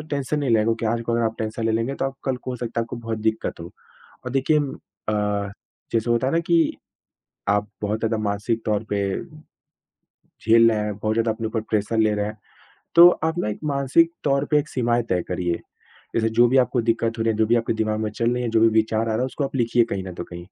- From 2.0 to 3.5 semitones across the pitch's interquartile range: Yes, narrow, 2.4 semitones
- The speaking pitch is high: No, low, 115 Hz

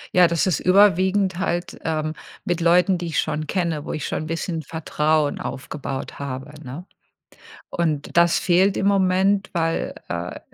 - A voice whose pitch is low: No, medium, 170 Hz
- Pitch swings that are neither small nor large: Yes, average, 3.3 semitones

